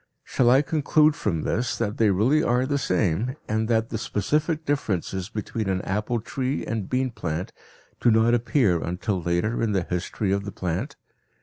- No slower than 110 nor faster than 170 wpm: No, average, 180 wpm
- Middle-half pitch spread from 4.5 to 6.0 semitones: Yes, average, 5.0 semitones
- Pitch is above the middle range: No, low, 110 Hz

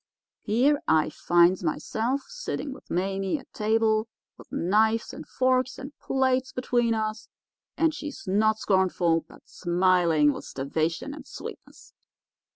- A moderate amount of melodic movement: No, wide, 6.4 semitones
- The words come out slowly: Yes, slow, 130 wpm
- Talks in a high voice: Yes, high, 215 Hz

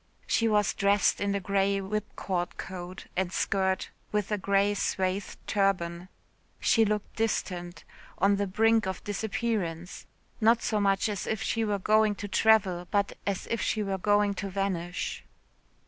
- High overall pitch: Yes, high, 200 Hz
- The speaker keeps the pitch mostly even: Yes, narrow, 1.9 semitones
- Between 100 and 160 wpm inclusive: Yes, average, 155 wpm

